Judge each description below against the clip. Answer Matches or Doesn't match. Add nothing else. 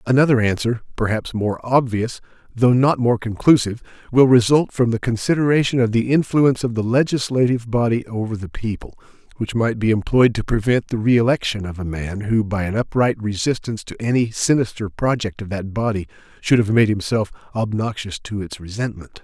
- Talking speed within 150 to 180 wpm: Matches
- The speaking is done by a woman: Doesn't match